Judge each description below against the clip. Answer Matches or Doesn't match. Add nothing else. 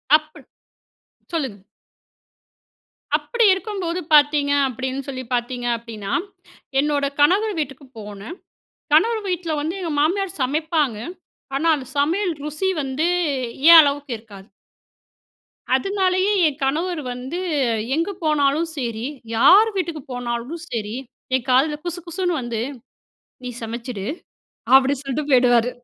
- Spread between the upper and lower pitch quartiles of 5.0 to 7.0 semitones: Matches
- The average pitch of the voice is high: Matches